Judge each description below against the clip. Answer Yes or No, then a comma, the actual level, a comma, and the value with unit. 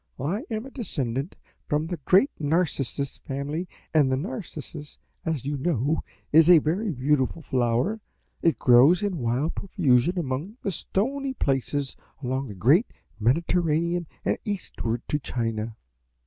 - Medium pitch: Yes, medium, 150 Hz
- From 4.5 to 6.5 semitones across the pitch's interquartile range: Yes, average, 5.3 semitones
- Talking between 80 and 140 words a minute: Yes, slow, 135 wpm